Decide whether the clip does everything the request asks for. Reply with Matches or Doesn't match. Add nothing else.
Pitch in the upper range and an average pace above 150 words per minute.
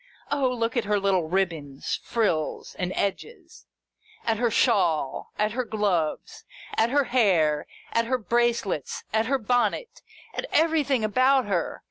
Doesn't match